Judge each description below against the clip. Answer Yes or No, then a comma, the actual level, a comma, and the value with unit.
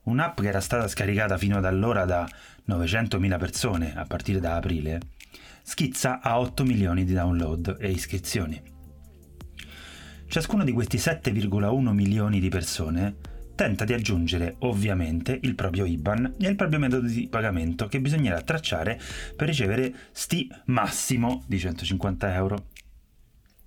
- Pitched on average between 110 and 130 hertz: No, low, 100 Hz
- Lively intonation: Yes, wide, 5.8 semitones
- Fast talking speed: No, average, 135 wpm